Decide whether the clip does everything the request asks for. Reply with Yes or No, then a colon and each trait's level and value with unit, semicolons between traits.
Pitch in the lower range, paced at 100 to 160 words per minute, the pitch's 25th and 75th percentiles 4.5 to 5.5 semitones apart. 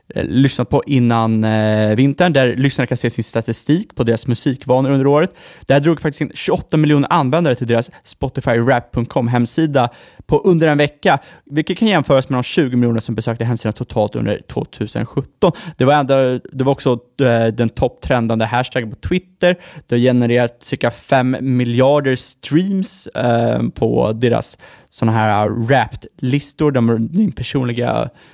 No: low, 130 Hz; average, 150 wpm; average, 3.7 semitones